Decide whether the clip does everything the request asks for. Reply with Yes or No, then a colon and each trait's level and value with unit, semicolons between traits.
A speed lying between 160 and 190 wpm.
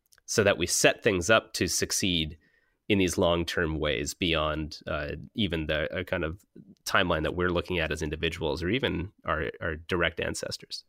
Yes: average, 180 wpm